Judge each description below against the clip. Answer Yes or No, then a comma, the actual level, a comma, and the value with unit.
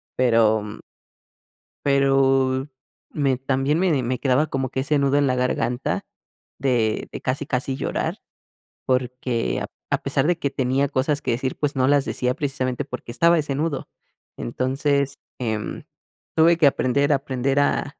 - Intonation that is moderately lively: No, narrow, 2.0 semitones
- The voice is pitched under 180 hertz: Yes, low, 135 Hz